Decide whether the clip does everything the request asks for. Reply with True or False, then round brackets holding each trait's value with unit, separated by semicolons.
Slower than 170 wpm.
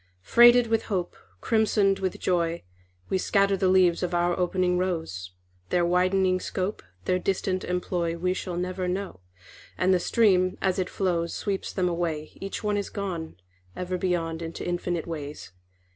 True (160 wpm)